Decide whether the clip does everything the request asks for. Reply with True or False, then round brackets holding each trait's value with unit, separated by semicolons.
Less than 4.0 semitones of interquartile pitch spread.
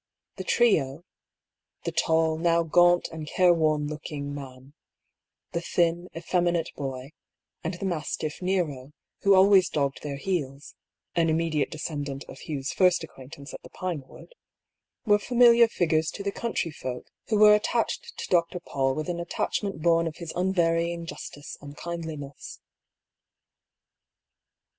True (3.4 semitones)